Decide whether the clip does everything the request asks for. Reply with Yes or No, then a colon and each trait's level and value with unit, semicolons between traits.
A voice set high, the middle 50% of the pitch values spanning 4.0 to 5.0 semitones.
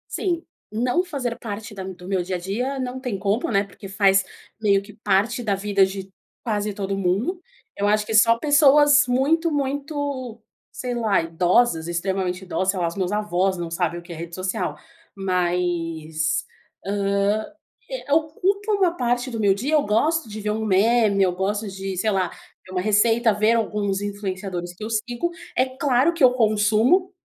Yes: high, 210 Hz; average, 4.6 semitones